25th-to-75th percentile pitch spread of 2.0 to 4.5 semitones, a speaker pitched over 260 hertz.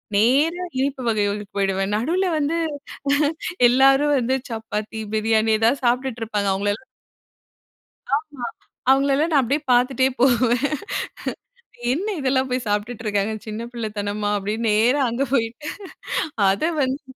No: average, 4.0 semitones; high, 240 Hz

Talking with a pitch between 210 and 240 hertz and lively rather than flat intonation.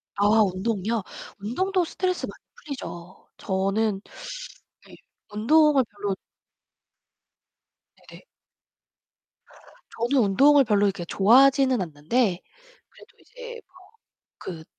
Yes: high, 220 Hz; wide, 6.0 semitones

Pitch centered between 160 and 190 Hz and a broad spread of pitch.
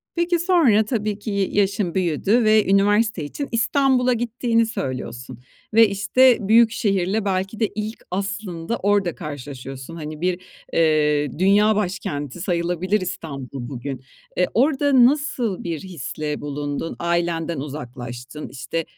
Yes: medium, 185 Hz; wide, 6.4 semitones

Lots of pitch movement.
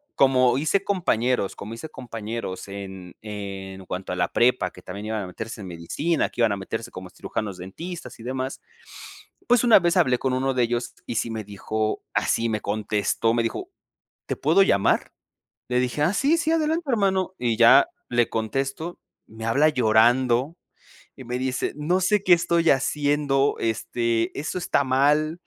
Yes: wide, 6.1 semitones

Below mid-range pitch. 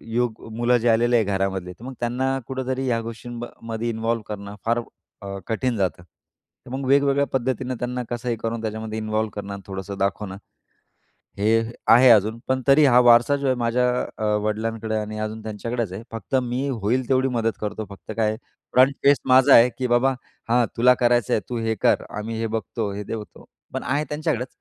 Yes: low, 115 Hz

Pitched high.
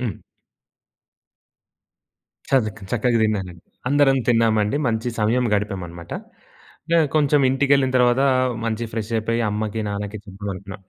No: low, 110 Hz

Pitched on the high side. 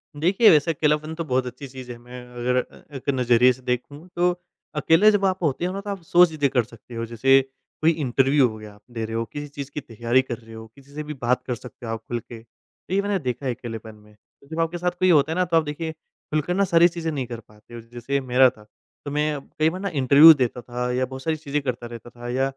No: low, 135 Hz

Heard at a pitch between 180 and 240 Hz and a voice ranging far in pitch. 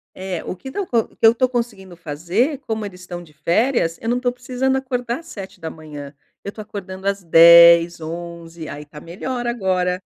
Yes: high, 190 Hz; wide, 6.0 semitones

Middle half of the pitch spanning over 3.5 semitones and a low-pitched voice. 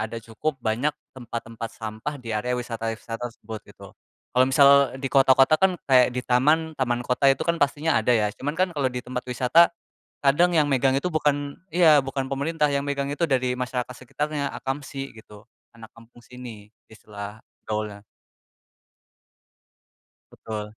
Yes: average, 4.0 semitones; low, 130 Hz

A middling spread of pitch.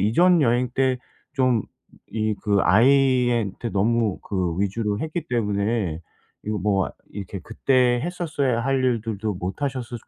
Yes: average, 4.1 semitones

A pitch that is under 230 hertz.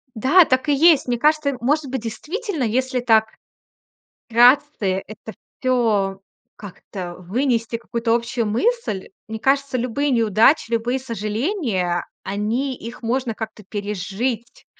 No: high, 235 Hz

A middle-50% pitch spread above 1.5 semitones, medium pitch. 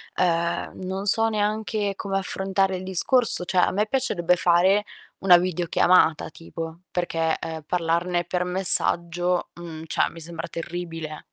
Yes: narrow, 2.4 semitones; medium, 180 Hz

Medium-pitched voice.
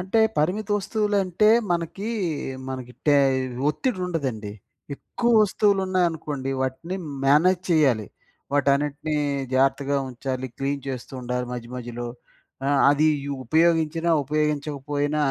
Yes: medium, 150 Hz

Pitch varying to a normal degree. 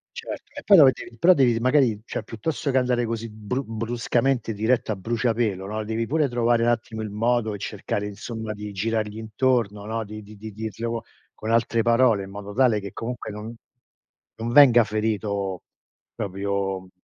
No: narrow, 2.3 semitones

